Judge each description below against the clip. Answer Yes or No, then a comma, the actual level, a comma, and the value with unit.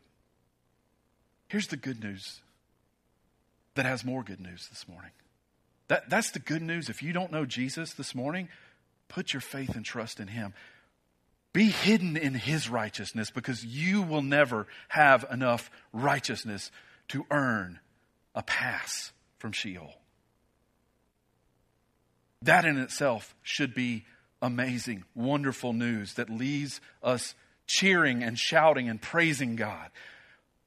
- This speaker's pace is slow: Yes, slow, 125 wpm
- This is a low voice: Yes, low, 125 Hz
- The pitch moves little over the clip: No, wide, 5.5 semitones